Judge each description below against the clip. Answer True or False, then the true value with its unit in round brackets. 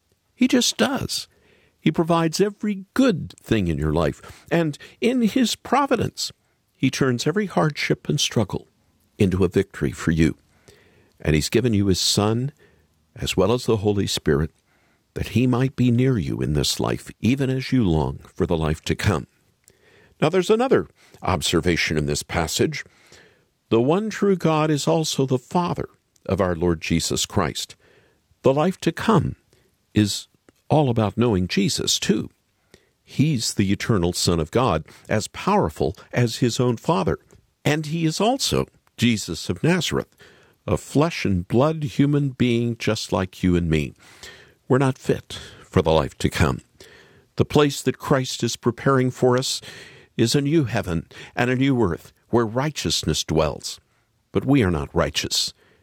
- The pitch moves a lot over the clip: True (7.7 semitones)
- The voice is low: True (120 Hz)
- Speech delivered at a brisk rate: False (160 wpm)